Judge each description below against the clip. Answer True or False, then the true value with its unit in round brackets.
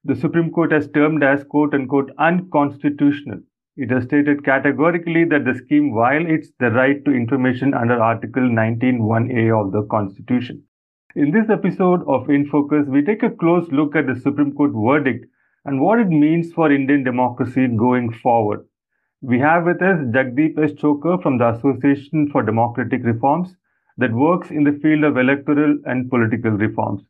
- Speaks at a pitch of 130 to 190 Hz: True (140 Hz)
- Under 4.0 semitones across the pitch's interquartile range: True (3.5 semitones)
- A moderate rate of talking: True (160 wpm)